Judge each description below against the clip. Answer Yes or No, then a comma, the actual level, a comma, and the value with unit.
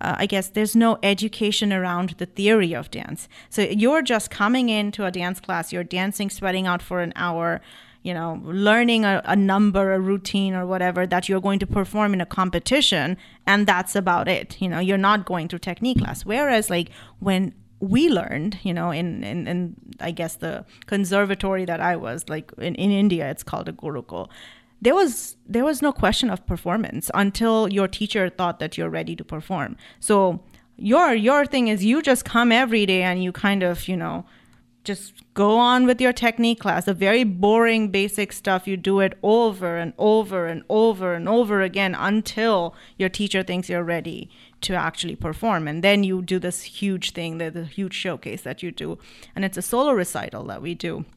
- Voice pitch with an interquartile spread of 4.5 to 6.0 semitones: No, average, 3.2 semitones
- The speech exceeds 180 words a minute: Yes, average, 195 wpm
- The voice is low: No, high, 195 Hz